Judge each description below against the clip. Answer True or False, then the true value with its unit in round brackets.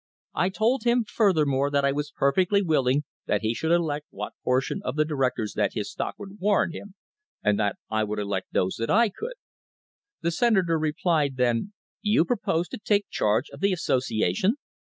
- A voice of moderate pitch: True (155 Hz)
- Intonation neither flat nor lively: False (7.8 semitones)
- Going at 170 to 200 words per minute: True (180 wpm)